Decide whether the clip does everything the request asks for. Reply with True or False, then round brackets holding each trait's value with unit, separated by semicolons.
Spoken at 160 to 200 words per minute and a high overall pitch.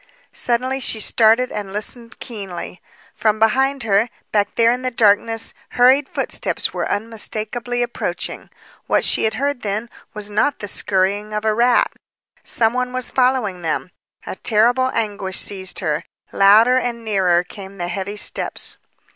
False (150 wpm; 220 Hz)